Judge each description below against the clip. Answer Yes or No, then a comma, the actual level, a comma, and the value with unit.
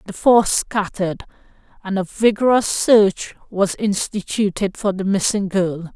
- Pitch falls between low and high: No, high, 200 Hz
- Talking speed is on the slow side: Yes, slow, 130 wpm